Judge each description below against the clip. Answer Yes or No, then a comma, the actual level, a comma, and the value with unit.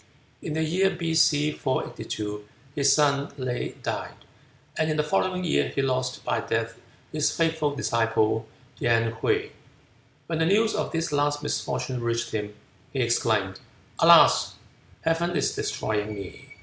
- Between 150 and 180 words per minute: No, average, 140 wpm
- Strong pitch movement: Yes, wide, 5.7 semitones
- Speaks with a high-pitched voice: No, medium, 140 Hz